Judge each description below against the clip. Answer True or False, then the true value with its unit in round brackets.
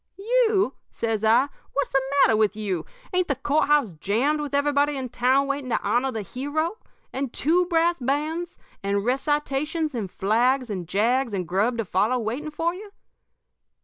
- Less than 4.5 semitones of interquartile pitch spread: False (5.3 semitones)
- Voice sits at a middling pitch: False (270 Hz)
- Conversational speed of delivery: True (170 wpm)